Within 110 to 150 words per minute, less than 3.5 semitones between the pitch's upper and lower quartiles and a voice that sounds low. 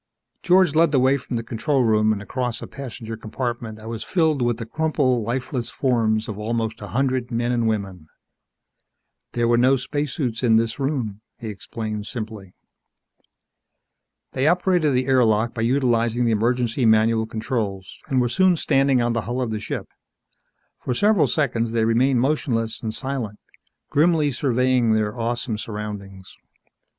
No: average, 160 wpm; average, 3.1 semitones; low, 120 Hz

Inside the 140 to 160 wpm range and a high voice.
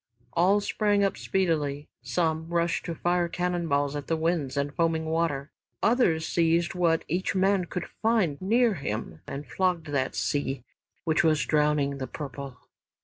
No: average, 155 wpm; medium, 165 Hz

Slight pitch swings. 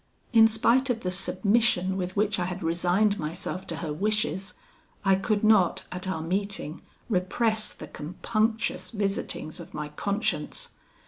No: average, 3.3 semitones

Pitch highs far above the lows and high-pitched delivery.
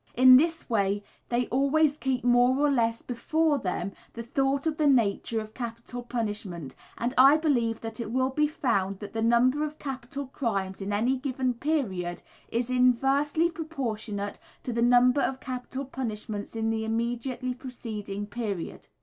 No: average, 3.4 semitones; high, 245 Hz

